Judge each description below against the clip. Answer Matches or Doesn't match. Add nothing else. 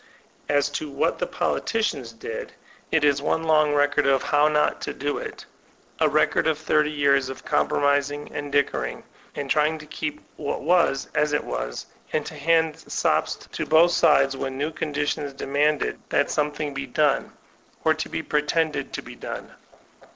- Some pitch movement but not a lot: Doesn't match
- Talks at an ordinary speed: Matches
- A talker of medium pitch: Matches